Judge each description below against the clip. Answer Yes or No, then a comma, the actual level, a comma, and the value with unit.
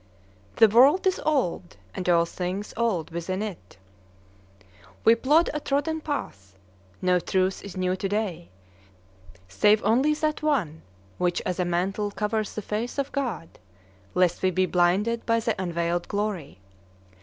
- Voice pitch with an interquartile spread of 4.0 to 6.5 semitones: Yes, average, 4.8 semitones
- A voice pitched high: Yes, high, 200 Hz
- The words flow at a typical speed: Yes, average, 145 wpm